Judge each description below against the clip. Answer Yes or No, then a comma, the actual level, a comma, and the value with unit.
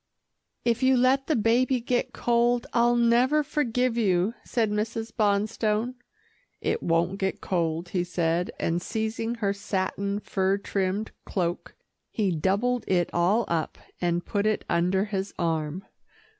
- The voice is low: No, high, 205 Hz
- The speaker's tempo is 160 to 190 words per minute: No, average, 140 wpm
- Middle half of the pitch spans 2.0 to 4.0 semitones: No, average, 4.6 semitones